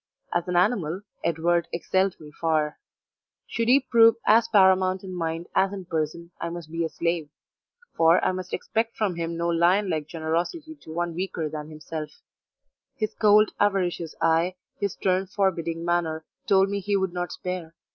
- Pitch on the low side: No, medium, 175 Hz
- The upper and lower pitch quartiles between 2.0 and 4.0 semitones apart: Yes, average, 2.9 semitones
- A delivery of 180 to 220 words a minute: No, average, 170 wpm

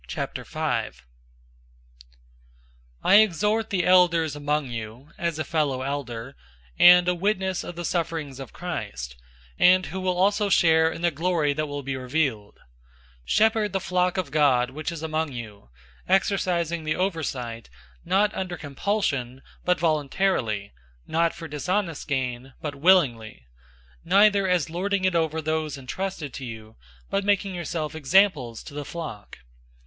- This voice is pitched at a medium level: Yes, medium, 160 Hz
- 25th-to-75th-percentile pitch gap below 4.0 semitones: No, average, 5.0 semitones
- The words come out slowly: No, average, 145 wpm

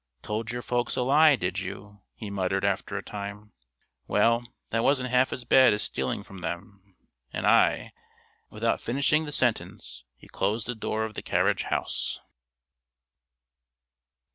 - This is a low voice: Yes, low, 110 Hz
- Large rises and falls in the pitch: No, average, 3.8 semitones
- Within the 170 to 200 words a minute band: No, average, 155 wpm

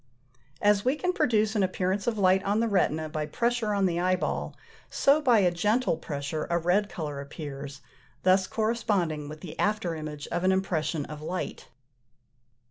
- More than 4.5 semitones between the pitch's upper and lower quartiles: Yes, average, 5.2 semitones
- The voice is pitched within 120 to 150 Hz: No, medium, 185 Hz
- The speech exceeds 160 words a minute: Yes, average, 170 wpm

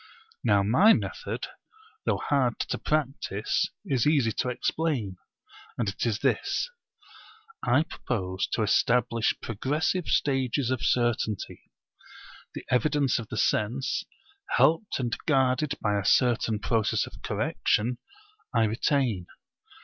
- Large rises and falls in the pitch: No, average, 4.1 semitones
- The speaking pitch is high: No, low, 125 Hz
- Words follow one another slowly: Yes, slow, 120 wpm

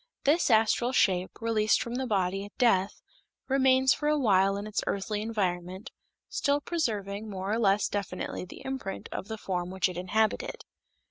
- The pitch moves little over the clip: No, average, 3.9 semitones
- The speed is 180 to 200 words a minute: No, average, 170 wpm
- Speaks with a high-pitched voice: Yes, high, 210 Hz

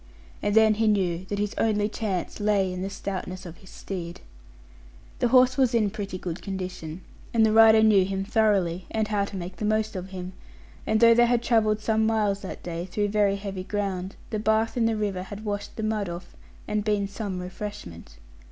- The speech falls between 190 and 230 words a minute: Yes, fast, 205 wpm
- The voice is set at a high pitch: Yes, high, 205 Hz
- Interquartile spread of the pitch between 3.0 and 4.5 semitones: No, narrow, 2.6 semitones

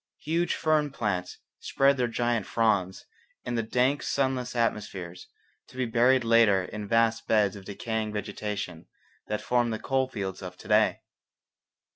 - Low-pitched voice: Yes, low, 115 Hz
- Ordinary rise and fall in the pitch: Yes, average, 3.6 semitones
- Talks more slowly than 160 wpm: Yes, average, 150 wpm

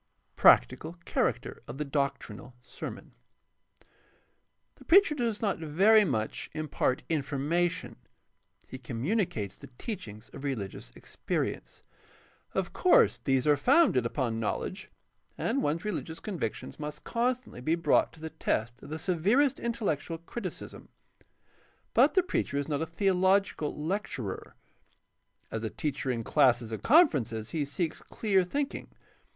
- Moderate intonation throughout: No, wide, 7.6 semitones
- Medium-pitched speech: Yes, medium, 155 Hz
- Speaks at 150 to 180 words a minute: No, slow, 135 wpm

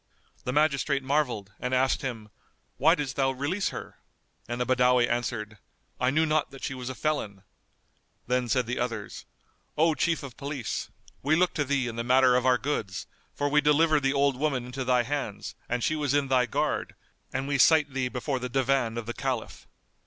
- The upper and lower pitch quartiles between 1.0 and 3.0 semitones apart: Yes, average, 2.7 semitones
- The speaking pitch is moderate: No, low, 130 Hz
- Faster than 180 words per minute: Yes, average, 195 wpm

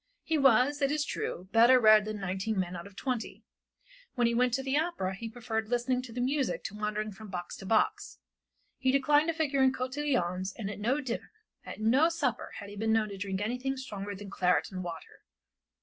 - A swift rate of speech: Yes, fast, 210 wpm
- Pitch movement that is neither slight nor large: Yes, average, 4.7 semitones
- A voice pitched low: No, high, 225 Hz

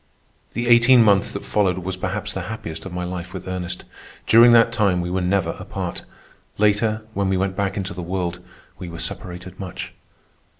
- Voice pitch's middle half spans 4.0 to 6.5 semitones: No, average, 2.9 semitones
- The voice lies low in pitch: Yes, very low, 95 Hz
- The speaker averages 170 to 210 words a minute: Yes, average, 185 wpm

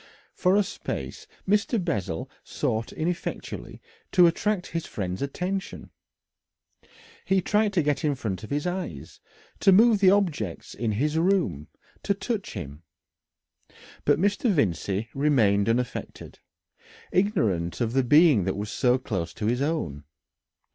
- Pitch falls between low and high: Yes, medium, 145 Hz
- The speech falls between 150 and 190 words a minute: No, slow, 135 wpm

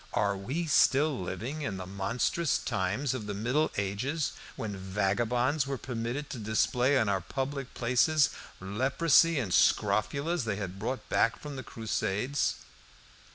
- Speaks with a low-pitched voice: Yes, low, 120 Hz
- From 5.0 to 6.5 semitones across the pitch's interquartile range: Yes, wide, 5.6 semitones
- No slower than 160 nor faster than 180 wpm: No, average, 145 wpm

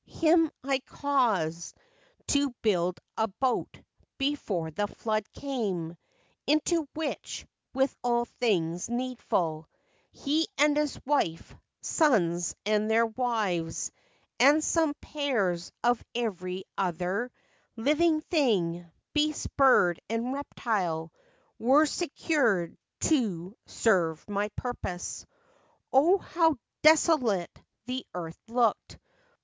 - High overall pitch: Yes, high, 235 Hz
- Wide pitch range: Yes, wide, 7.9 semitones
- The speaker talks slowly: Yes, slow, 100 wpm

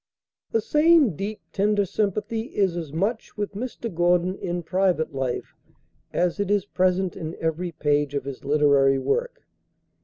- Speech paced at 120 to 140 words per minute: No, average, 150 wpm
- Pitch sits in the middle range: Yes, medium, 180 Hz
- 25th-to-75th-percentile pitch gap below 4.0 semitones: No, average, 4.8 semitones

